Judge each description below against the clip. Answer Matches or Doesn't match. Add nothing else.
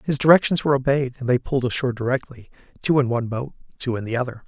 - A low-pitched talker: Matches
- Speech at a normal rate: Doesn't match